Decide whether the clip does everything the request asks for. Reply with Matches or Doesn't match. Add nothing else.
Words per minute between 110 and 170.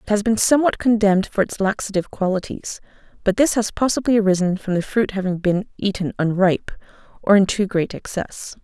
Doesn't match